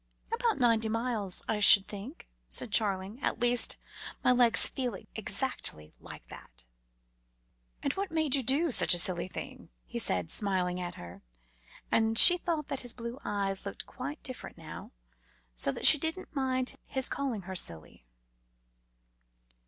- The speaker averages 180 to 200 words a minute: No, average, 150 wpm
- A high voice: Yes, high, 230 Hz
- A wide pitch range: Yes, wide, 5.7 semitones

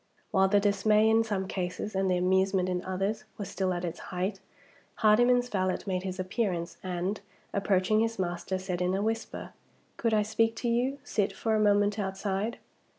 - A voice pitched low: No, high, 195 Hz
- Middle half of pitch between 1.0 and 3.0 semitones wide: Yes, average, 2.7 semitones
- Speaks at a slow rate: No, average, 180 wpm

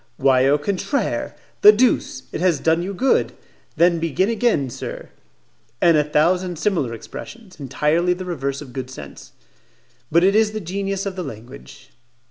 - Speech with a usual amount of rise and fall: No, wide, 5.8 semitones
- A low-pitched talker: No, medium, 170 Hz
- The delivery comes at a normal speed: Yes, average, 160 wpm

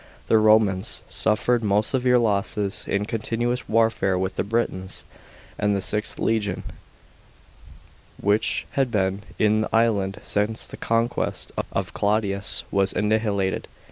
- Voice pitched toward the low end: Yes, low, 105 Hz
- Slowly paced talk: Yes, slow, 130 wpm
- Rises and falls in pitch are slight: Yes, narrow, 2.3 semitones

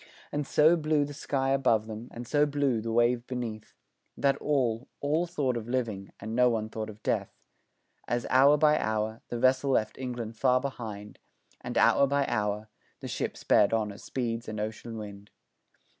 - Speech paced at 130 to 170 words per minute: No, average, 180 wpm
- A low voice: Yes, low, 120 Hz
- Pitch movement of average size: Yes, average, 3.9 semitones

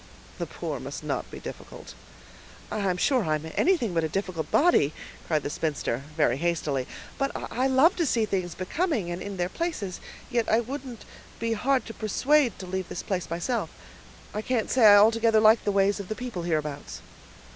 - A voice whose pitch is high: Yes, high, 205 Hz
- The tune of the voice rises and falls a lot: Yes, wide, 6.1 semitones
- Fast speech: No, average, 185 wpm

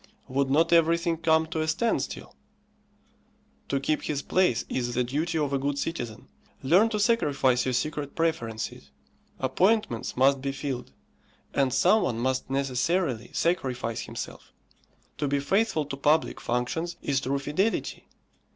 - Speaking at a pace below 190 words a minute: Yes, average, 140 wpm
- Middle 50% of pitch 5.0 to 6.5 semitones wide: No, average, 4.1 semitones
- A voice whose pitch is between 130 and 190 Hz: Yes, medium, 140 Hz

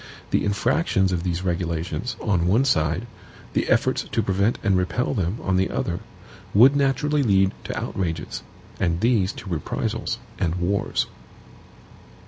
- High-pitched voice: No, very low, 95 Hz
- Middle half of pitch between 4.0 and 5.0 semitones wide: Yes, average, 4.6 semitones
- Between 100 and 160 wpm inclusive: Yes, average, 140 wpm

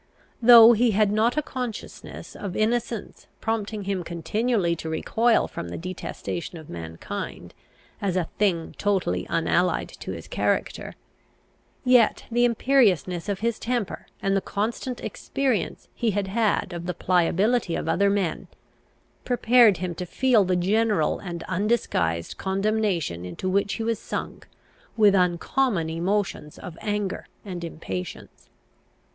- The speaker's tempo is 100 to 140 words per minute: Yes, slow, 135 wpm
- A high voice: Yes, high, 200 Hz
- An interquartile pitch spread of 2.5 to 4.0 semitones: No, average, 4.5 semitones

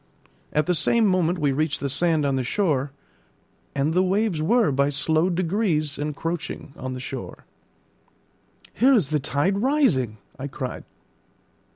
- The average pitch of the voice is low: No, medium, 155 Hz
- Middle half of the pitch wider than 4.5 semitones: Yes, average, 5.0 semitones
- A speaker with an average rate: Yes, average, 150 wpm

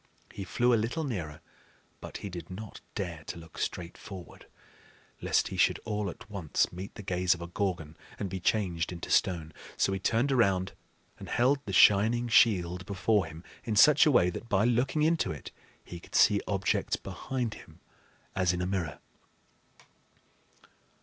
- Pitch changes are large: No, average, 4.3 semitones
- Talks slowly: No, average, 175 wpm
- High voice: No, very low, 95 Hz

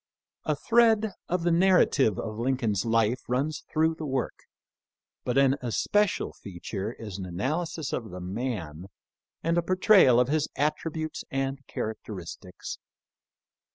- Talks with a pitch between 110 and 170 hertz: Yes, low, 135 Hz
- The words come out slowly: Yes, slow, 130 wpm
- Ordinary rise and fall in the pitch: No, wide, 6.7 semitones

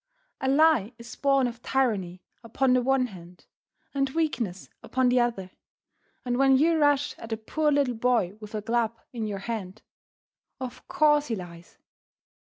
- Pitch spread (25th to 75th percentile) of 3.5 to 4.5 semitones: Yes, average, 4.0 semitones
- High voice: Yes, high, 245 Hz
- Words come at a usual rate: Yes, average, 165 wpm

